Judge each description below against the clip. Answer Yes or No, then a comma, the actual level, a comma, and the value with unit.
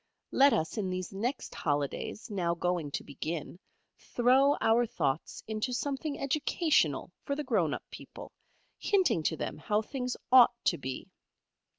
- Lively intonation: Yes, wide, 8.1 semitones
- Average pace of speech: Yes, average, 150 wpm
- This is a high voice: Yes, high, 215 Hz